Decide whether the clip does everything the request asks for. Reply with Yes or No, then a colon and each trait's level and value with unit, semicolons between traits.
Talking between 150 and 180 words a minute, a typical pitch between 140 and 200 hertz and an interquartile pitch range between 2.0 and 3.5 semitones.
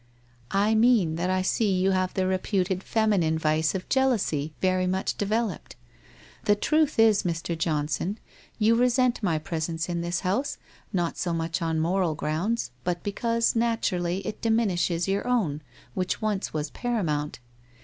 No: average, 160 wpm; medium, 185 Hz; average, 4.8 semitones